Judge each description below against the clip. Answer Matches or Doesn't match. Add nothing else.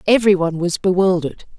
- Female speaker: Matches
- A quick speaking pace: Doesn't match